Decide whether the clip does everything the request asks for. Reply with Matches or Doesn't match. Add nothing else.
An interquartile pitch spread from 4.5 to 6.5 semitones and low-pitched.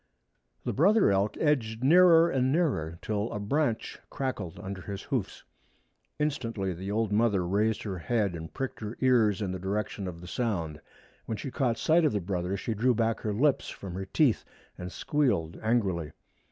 Matches